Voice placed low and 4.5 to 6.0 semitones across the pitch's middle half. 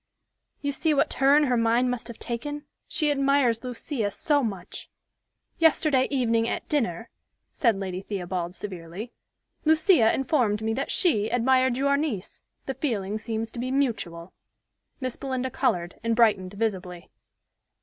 No: high, 235 Hz; average, 4.9 semitones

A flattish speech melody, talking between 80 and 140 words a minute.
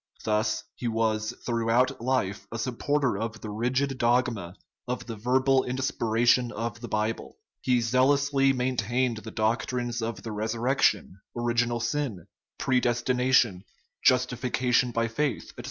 Yes: narrow, 2.3 semitones; slow, 135 wpm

